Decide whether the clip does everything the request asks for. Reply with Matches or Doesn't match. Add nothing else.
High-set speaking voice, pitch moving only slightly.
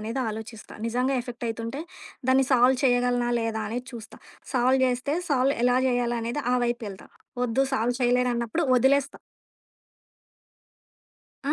Matches